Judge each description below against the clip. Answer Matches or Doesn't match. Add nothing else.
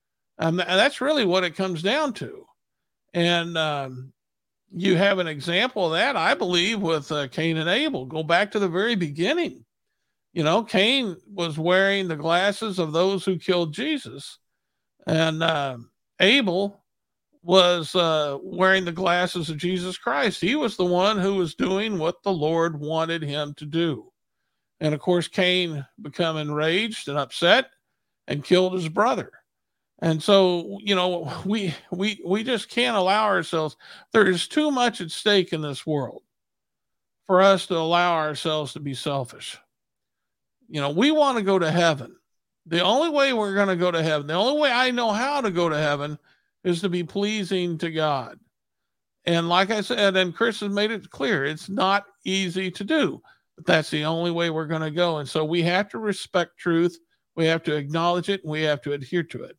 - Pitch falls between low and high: Matches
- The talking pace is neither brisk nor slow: Matches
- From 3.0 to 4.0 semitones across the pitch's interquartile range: Matches